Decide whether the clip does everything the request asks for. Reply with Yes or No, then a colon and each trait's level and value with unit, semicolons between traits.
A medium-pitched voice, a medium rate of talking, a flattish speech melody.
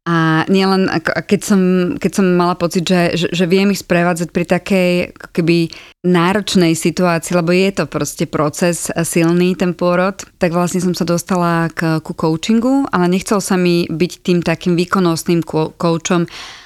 Yes: medium, 175 Hz; average, 155 wpm; narrow, 1.6 semitones